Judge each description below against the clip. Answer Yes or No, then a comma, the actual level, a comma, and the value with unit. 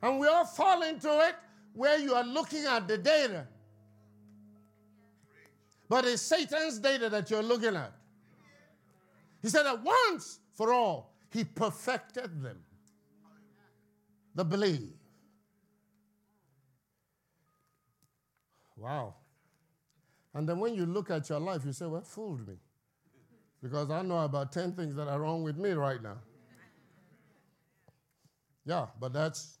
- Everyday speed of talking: No, slow, 130 wpm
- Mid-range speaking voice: Yes, medium, 160 Hz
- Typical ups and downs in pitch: No, wide, 8.6 semitones